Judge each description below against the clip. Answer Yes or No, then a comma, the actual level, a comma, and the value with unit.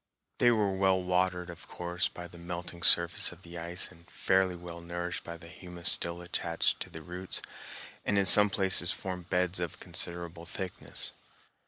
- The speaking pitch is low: Yes, very low, 90 Hz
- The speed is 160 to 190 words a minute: Yes, average, 170 wpm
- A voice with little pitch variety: Yes, narrow, 1.3 semitones